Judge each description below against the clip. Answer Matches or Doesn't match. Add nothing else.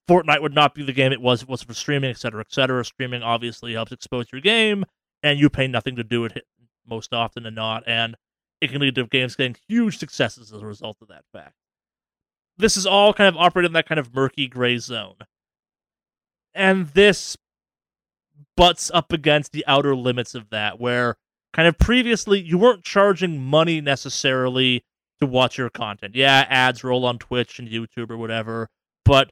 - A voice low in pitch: Matches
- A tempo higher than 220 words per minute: Doesn't match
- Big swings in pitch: Doesn't match